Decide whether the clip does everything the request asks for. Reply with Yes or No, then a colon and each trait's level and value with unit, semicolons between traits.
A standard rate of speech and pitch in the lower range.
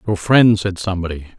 Yes: average, 175 wpm; very low, 95 Hz